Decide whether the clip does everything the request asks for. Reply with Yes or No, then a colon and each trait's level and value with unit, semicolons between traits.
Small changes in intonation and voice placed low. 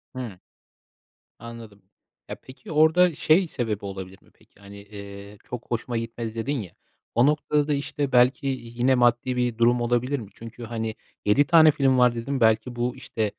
No: average, 3.2 semitones; low, 120 Hz